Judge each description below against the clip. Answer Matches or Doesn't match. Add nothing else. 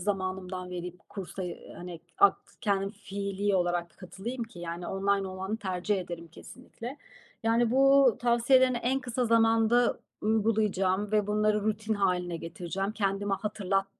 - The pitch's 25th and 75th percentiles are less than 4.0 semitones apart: Matches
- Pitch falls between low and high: Doesn't match